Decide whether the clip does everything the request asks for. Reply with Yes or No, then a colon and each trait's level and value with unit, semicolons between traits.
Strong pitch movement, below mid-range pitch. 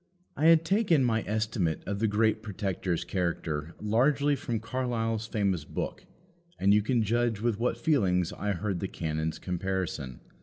No: average, 4.7 semitones; low, 105 Hz